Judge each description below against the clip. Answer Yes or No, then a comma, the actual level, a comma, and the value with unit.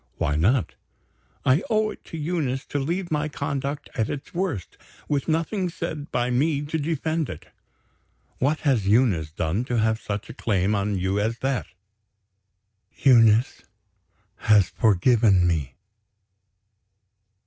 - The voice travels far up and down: Yes, wide, 6.5 semitones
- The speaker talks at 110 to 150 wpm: Yes, slow, 135 wpm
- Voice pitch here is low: Yes, low, 125 Hz